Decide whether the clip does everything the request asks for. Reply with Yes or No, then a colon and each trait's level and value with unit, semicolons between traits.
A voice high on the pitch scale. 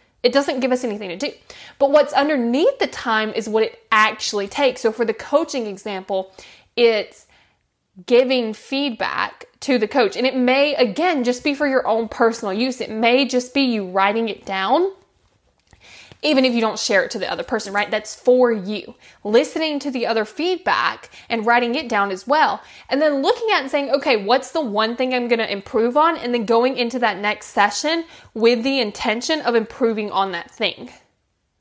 Yes: high, 240 Hz